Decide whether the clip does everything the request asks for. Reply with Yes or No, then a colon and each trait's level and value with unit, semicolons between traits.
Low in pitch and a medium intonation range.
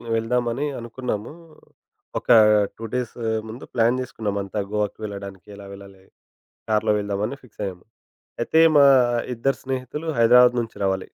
Yes: low, 115 Hz; average, 3.5 semitones